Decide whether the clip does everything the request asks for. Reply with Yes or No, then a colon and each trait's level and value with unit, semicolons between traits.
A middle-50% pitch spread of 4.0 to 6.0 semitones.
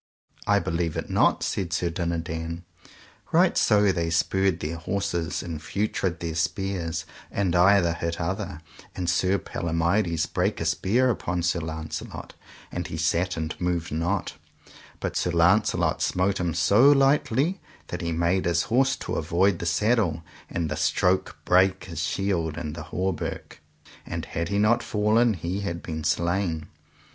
No: average, 3.2 semitones